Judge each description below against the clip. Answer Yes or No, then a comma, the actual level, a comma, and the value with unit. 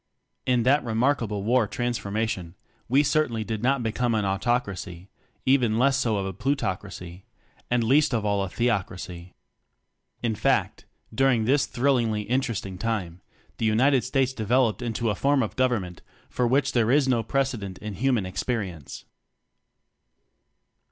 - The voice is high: No, low, 115 Hz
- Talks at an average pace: Yes, average, 145 wpm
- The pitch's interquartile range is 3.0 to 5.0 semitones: Yes, average, 4.2 semitones